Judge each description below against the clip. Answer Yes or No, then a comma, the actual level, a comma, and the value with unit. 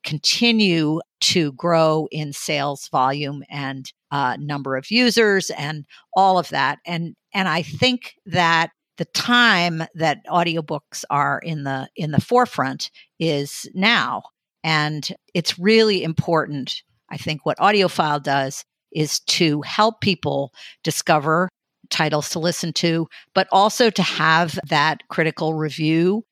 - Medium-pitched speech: Yes, medium, 160 Hz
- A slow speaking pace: Yes, slow, 130 wpm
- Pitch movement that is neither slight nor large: Yes, average, 3.5 semitones